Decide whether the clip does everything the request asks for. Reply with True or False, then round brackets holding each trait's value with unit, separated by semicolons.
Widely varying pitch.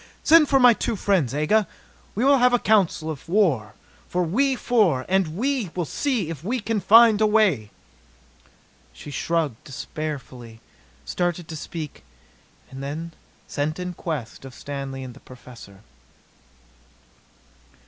True (7.6 semitones)